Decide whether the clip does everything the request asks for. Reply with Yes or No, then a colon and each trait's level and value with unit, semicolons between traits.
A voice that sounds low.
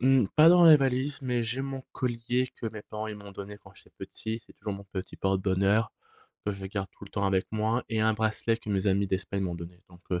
Yes: low, 110 Hz